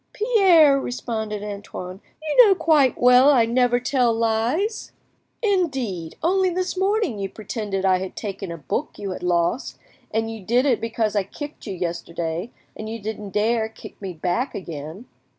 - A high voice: Yes, high, 225 Hz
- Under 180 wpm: Yes, average, 165 wpm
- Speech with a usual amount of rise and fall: No, wide, 6.1 semitones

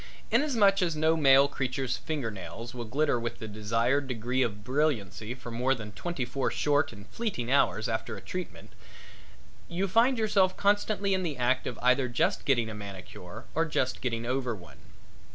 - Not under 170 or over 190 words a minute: Yes, average, 175 wpm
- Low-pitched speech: Yes, low, 130 Hz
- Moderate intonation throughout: No, wide, 5.7 semitones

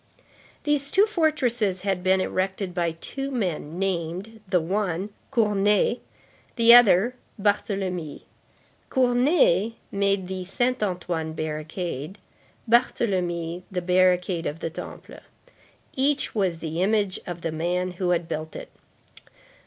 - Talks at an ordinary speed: No, slow, 120 wpm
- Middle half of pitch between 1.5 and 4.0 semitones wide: No, average, 4.4 semitones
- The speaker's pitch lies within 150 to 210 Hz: Yes, high, 190 Hz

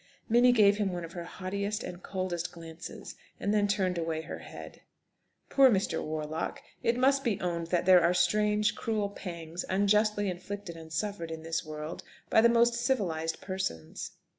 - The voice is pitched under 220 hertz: Yes, medium, 185 Hz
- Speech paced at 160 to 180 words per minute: Yes, average, 170 wpm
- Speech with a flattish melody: No, average, 4.0 semitones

